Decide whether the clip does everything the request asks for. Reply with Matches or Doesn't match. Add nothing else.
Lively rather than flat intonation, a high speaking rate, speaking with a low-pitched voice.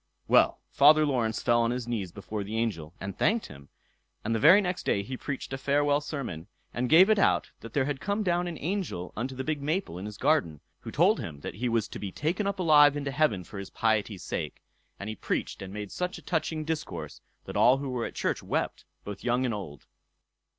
Matches